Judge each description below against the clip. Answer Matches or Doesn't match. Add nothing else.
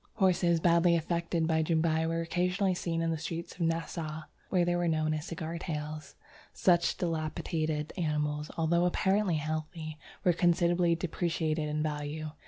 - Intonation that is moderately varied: Doesn't match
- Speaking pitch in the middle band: Matches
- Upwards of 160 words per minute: Doesn't match